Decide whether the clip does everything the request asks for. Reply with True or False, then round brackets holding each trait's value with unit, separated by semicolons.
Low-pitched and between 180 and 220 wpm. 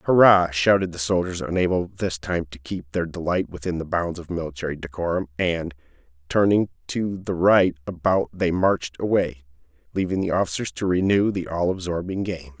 False (85 Hz; 165 wpm)